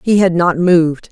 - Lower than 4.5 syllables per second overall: No, 5.0 syllables/s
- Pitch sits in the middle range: Yes, medium, 175 Hz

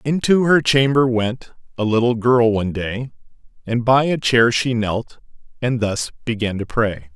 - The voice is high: No, low, 120 Hz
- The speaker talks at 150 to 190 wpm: Yes, average, 170 wpm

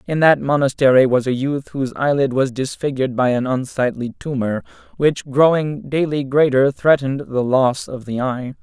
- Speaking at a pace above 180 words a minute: No, average, 165 wpm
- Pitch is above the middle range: No, low, 135 Hz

